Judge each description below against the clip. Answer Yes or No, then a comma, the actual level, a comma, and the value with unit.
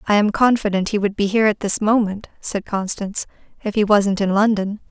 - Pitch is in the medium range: No, high, 205 Hz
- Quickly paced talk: Yes, fast, 210 wpm